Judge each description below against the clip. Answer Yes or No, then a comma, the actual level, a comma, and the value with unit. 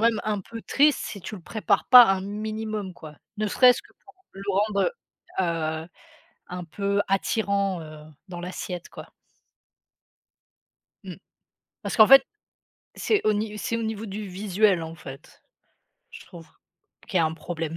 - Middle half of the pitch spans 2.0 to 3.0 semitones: No, average, 3.7 semitones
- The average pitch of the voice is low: No, high, 200 Hz